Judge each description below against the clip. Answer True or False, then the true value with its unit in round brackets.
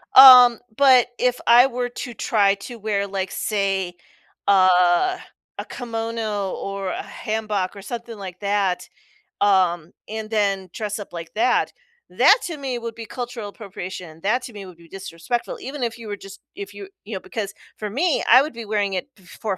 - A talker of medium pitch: False (210 Hz)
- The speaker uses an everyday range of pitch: True (3.6 semitones)